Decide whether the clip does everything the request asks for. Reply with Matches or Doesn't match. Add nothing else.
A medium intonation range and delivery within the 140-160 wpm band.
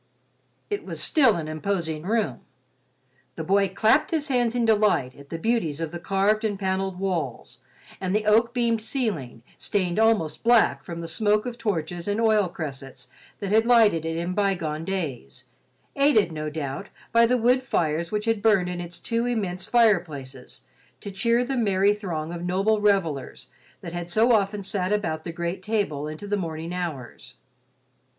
Doesn't match